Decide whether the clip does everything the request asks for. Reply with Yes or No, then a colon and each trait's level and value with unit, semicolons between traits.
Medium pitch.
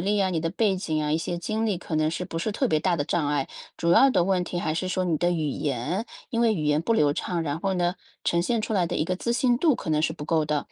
Yes: medium, 175 Hz